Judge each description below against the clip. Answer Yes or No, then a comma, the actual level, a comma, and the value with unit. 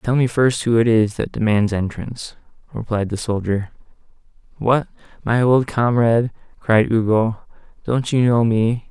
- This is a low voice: Yes, low, 115 Hz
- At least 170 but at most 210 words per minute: No, average, 150 wpm